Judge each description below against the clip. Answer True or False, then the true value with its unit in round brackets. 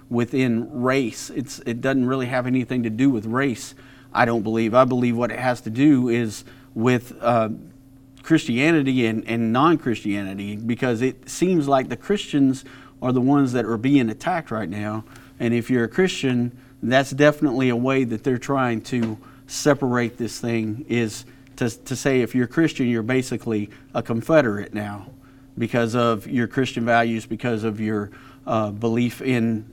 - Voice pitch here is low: True (125 Hz)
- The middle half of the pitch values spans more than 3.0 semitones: False (2.5 semitones)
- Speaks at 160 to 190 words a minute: True (170 wpm)